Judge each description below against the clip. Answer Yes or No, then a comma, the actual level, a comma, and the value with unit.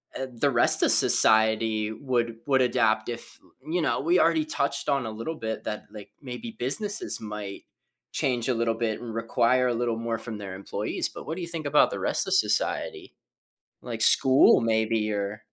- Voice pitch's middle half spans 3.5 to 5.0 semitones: Yes, average, 4.1 semitones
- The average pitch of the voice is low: Yes, low, 120 Hz